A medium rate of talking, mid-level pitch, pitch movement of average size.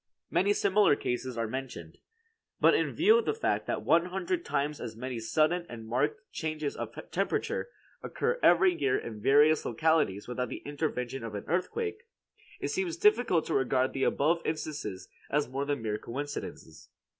No: average, 170 wpm; medium, 145 Hz; wide, 6.3 semitones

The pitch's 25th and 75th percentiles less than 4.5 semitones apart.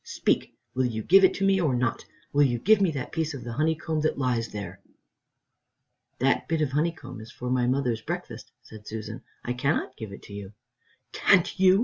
No: wide, 5.6 semitones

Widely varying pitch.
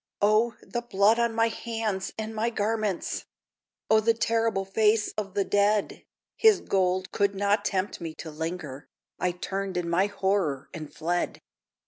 No: average, 3.3 semitones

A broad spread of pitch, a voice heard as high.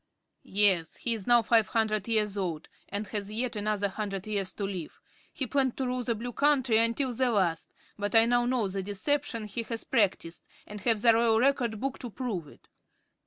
No: average, 3.2 semitones; high, 220 Hz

